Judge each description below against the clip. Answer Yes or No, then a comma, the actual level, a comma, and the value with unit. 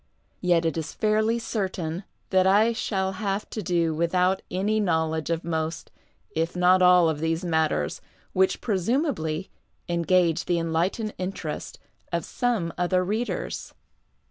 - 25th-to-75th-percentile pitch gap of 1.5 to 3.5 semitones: Yes, average, 3.1 semitones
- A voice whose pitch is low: No, medium, 180 Hz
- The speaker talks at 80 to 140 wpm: Yes, slow, 135 wpm